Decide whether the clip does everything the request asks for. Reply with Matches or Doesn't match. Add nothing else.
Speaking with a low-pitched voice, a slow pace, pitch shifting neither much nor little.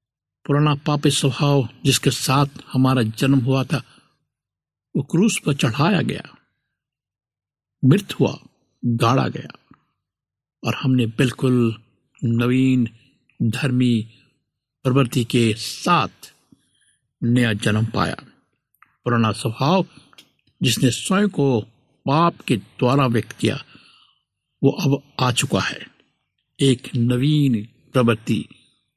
Matches